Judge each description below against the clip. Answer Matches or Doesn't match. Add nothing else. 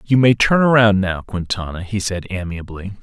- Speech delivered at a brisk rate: Doesn't match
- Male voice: Matches